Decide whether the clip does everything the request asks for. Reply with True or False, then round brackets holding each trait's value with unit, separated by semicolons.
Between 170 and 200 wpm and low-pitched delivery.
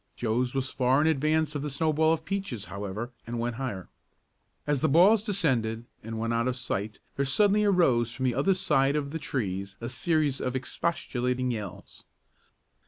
True (175 wpm; 130 Hz)